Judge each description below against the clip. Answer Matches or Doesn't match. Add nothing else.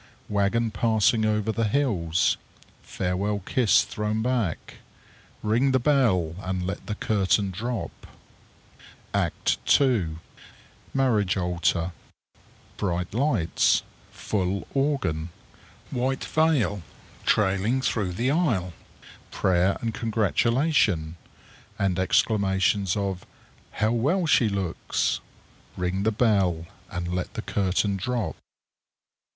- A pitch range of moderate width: Matches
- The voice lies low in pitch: Matches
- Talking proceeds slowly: Matches